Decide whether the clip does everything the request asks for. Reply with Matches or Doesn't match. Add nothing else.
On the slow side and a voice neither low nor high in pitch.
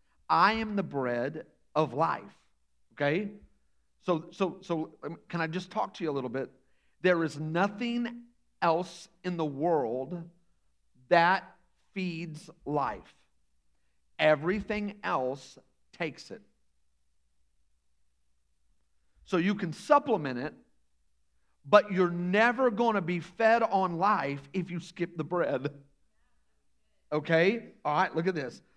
Matches